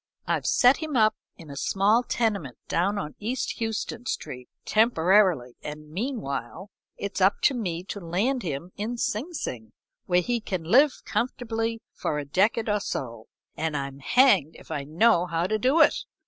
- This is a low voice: No, high, 200 Hz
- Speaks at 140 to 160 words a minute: No, average, 170 wpm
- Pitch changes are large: Yes, wide, 6.7 semitones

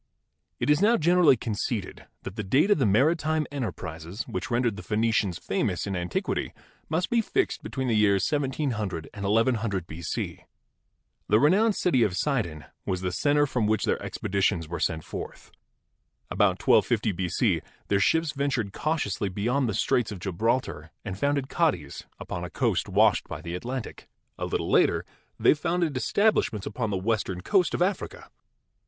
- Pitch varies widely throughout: Yes, wide, 7.1 semitones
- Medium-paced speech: Yes, average, 165 wpm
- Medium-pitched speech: No, low, 115 Hz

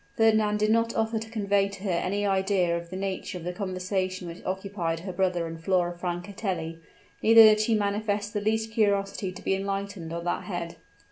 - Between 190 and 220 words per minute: Yes, average, 195 wpm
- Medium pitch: No, high, 195 Hz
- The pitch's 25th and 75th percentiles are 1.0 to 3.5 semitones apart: Yes, average, 2.8 semitones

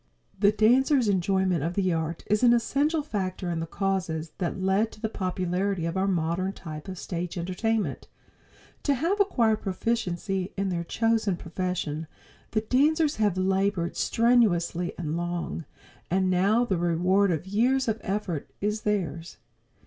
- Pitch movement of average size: Yes, average, 4.0 semitones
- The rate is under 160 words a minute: Yes, average, 150 wpm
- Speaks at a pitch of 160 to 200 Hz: Yes, high, 190 Hz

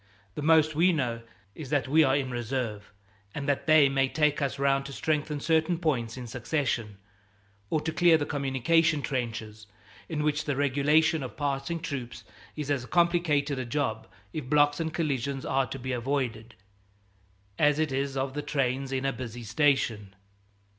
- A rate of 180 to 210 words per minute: No, average, 170 wpm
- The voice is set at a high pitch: No, medium, 140 Hz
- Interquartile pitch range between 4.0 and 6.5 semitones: No, average, 3.0 semitones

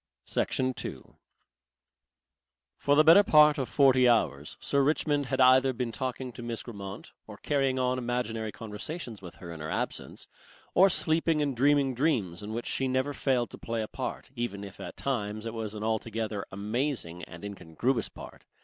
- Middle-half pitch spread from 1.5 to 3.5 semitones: No, average, 4.2 semitones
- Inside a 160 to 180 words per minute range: Yes, average, 175 wpm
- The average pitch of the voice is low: Yes, low, 120 Hz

